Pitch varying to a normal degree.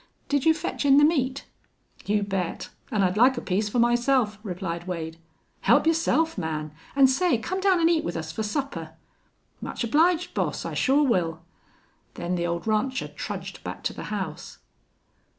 No: wide, 8.1 semitones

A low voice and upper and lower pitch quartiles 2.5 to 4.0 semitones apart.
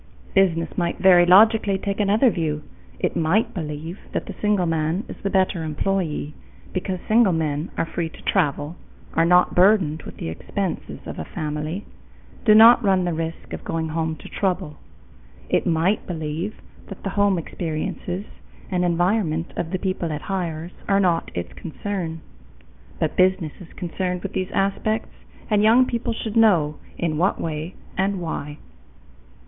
No: medium, 180 Hz; average, 3.5 semitones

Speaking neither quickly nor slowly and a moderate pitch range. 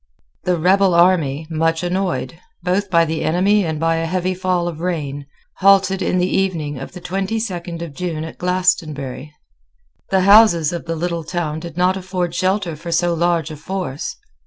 No: average, 180 wpm; narrow, 2.3 semitones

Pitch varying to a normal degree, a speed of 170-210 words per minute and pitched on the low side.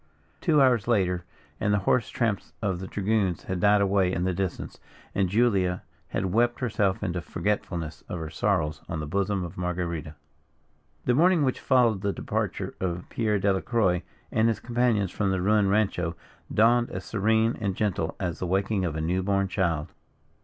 Yes: average, 3.6 semitones; average, 175 wpm; low, 100 Hz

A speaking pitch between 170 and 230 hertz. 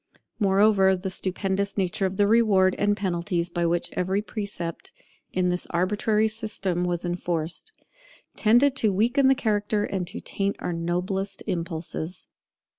Yes: high, 190 Hz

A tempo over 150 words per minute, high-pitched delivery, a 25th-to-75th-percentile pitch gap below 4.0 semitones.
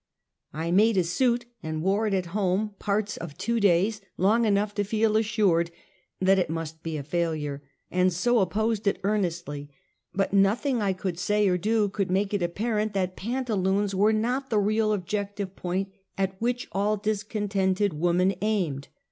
Yes: average, 165 wpm; high, 200 Hz; average, 3.0 semitones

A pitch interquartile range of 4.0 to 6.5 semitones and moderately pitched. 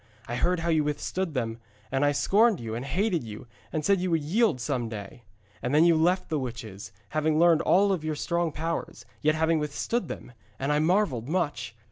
Yes: average, 5.2 semitones; medium, 155 Hz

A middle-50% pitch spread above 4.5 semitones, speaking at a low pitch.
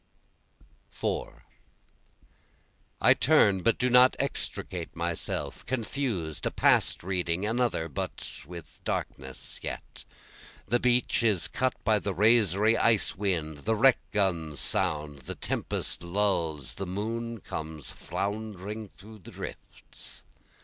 Yes: average, 5.2 semitones; low, 100 Hz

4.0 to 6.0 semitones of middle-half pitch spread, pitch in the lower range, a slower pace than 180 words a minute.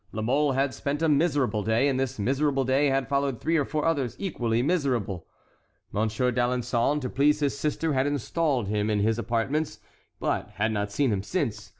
No: average, 4.3 semitones; low, 130 Hz; average, 190 wpm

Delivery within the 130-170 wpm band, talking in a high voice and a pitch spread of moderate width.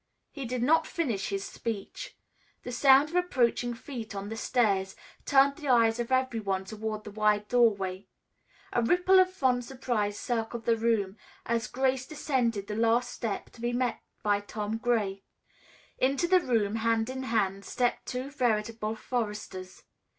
Yes: average, 160 wpm; high, 230 Hz; average, 3.6 semitones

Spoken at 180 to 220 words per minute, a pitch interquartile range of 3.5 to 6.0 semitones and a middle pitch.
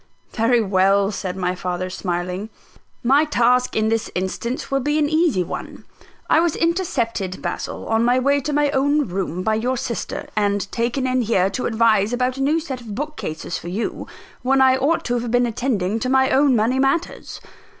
No: average, 190 wpm; average, 5.2 semitones; high, 240 Hz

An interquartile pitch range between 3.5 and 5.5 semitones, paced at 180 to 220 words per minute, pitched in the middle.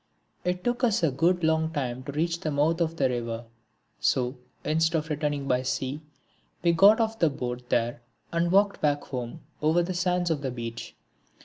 Yes: average, 4.8 semitones; average, 190 wpm; medium, 155 Hz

